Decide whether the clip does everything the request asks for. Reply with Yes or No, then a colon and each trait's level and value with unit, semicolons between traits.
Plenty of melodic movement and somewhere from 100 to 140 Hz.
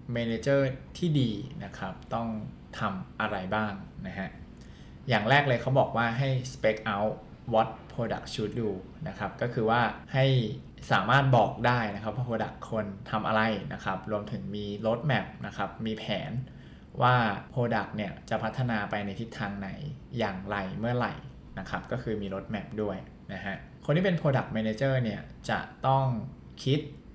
No: average, 3.2 semitones; low, 115 Hz